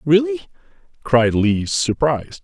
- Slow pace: Yes, slow, 100 wpm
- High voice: No, low, 135 Hz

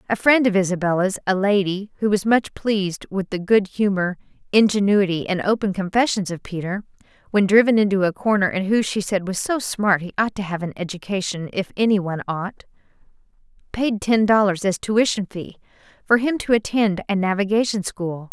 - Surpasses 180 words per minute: No, average, 175 wpm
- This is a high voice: Yes, high, 200 Hz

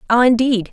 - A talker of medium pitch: No, high, 235 Hz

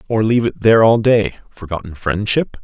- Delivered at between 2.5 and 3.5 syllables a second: No, 5.7 syllables/s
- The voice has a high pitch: No, low, 105 Hz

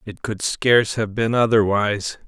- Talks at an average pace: Yes, average, 160 wpm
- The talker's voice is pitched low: Yes, low, 110 Hz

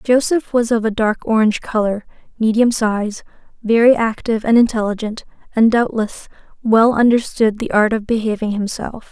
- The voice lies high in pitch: Yes, high, 225 Hz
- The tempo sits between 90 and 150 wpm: Yes, average, 145 wpm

